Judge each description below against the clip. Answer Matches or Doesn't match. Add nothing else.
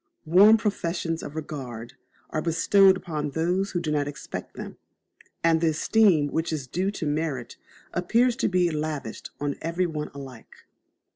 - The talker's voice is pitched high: Doesn't match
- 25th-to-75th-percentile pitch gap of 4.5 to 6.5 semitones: Doesn't match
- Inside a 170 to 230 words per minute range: Doesn't match